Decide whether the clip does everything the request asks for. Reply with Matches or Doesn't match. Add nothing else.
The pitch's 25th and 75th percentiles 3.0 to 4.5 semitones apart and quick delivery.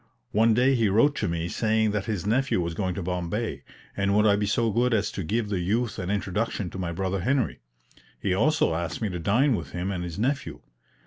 Matches